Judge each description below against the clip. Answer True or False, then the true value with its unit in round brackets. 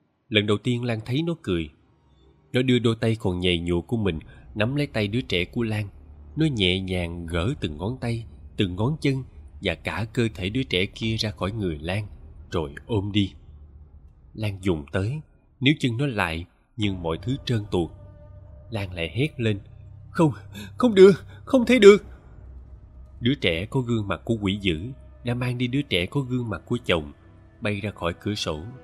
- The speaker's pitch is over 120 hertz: False (105 Hz)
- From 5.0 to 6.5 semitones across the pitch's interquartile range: True (5.6 semitones)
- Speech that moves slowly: False (190 wpm)